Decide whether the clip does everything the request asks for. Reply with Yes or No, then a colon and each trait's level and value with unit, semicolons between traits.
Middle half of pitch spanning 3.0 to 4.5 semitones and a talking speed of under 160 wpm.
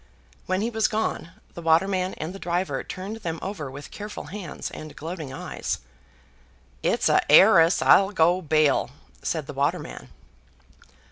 Yes: average, 3.6 semitones; average, 145 wpm